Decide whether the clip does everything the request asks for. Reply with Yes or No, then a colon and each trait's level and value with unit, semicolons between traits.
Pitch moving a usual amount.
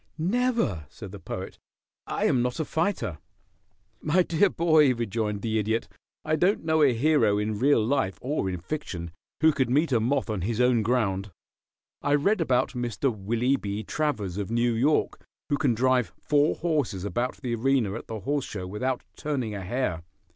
No: wide, 5.7 semitones